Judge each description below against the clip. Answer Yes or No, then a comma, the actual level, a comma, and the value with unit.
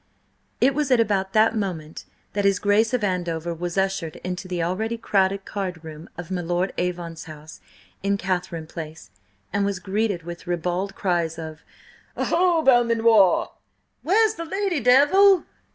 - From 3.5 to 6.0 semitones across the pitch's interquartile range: Yes, average, 4.6 semitones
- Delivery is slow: No, average, 155 wpm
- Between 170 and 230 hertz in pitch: Yes, high, 190 Hz